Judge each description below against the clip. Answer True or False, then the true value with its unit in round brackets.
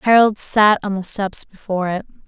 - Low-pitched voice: False (200 Hz)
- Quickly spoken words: False (185 wpm)